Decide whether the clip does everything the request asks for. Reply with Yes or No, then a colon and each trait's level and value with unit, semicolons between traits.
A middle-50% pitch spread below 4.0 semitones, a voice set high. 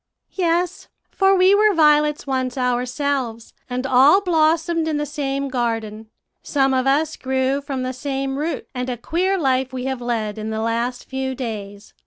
Yes: average, 3.6 semitones; very high, 265 Hz